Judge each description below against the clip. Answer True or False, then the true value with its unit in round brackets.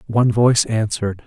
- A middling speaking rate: True (145 wpm)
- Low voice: True (110 Hz)